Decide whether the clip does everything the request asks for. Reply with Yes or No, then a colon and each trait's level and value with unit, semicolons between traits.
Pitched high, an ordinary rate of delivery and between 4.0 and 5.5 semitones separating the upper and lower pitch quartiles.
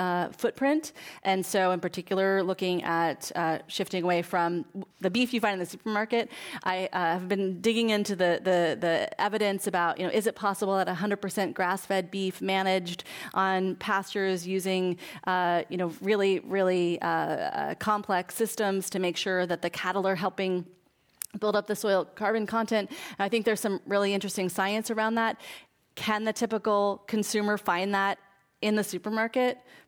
No: high, 195 Hz; average, 170 wpm; narrow, 2.6 semitones